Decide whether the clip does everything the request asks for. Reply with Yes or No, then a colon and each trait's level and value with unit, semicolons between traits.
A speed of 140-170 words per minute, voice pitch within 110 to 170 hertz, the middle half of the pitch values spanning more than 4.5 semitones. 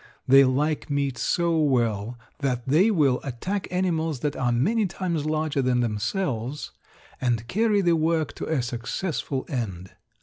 Yes: average, 145 wpm; medium, 140 Hz; average, 5.3 semitones